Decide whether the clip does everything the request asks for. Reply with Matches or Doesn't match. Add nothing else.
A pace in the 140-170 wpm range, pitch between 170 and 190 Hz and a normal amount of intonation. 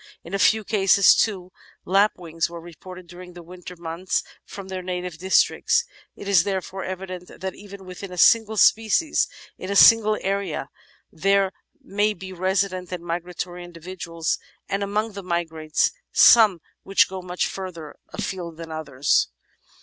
Doesn't match